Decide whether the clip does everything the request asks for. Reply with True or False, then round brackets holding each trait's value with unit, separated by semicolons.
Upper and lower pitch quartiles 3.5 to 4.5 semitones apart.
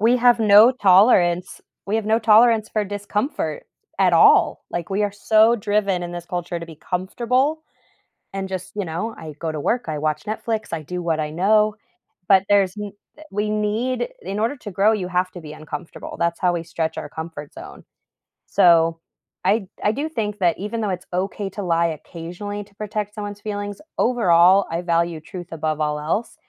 True (3.9 semitones)